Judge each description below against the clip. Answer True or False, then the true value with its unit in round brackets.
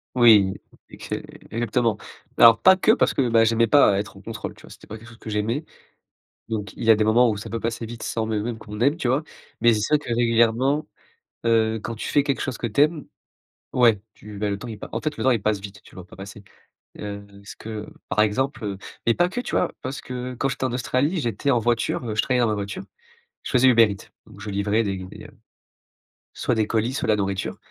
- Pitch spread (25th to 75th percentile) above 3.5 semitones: False (3.1 semitones)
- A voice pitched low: True (115 Hz)